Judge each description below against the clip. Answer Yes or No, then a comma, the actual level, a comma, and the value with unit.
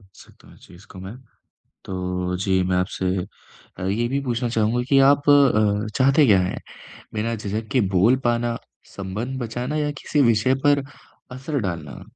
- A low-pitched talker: Yes, low, 115 Hz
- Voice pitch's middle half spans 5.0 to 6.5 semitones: Yes, average, 5.3 semitones